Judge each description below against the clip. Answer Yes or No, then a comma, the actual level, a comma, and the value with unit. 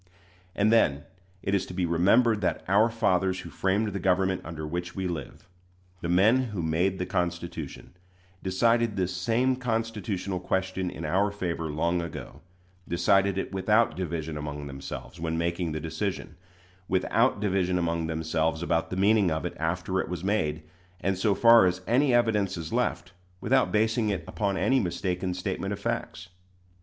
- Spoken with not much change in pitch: No, average, 3.5 semitones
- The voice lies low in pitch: Yes, very low, 95 Hz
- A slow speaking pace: No, average, 165 wpm